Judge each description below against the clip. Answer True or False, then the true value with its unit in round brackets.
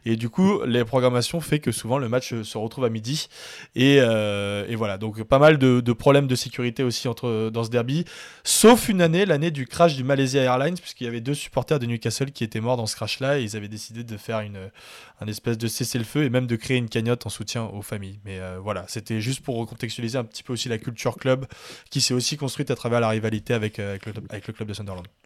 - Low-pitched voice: True (120 Hz)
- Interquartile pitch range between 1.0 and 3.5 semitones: True (3.2 semitones)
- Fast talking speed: True (250 wpm)